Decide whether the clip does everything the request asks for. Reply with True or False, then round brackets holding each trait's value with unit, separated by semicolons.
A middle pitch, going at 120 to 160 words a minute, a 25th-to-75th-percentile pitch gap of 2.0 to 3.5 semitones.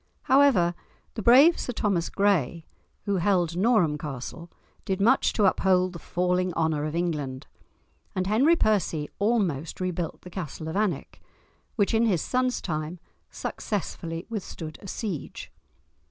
False (180 Hz; 140 wpm; 4.4 semitones)